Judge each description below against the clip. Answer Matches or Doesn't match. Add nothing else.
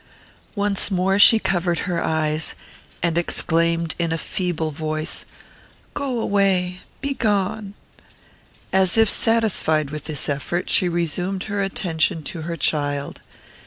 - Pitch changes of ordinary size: Matches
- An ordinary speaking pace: Doesn't match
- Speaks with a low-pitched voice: Doesn't match